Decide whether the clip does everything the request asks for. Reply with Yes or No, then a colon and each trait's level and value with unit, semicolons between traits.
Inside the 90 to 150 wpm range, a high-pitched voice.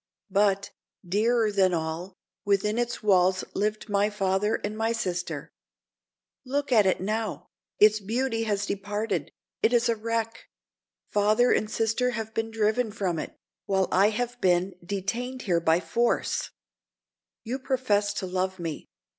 Yes: average, 140 wpm; high, 210 Hz